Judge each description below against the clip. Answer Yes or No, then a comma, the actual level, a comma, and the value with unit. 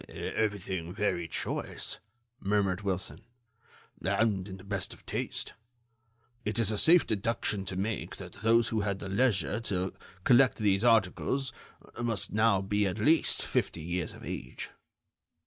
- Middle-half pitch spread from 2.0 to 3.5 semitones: Yes, average, 2.9 semitones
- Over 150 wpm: No, average, 145 wpm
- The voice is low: Yes, low, 100 Hz